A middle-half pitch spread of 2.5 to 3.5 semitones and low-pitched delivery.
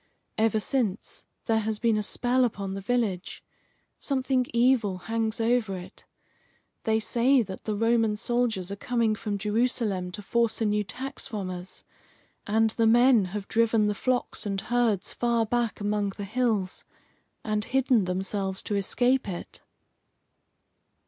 No: average, 3.0 semitones; high, 220 Hz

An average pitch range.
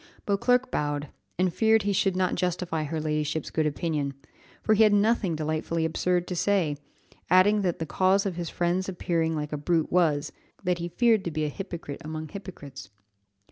Yes: average, 3.7 semitones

